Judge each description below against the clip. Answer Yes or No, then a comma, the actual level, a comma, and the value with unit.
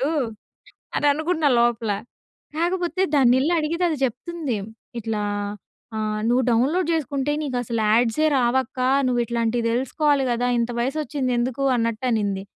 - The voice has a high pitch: Yes, very high, 255 Hz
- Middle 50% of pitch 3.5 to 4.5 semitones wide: Yes, average, 4.2 semitones